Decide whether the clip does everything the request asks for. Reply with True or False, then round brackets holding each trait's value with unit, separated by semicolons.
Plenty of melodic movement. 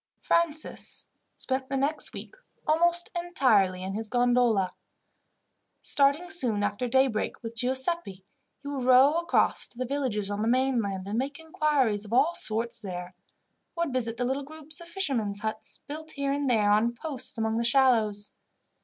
False (4.8 semitones)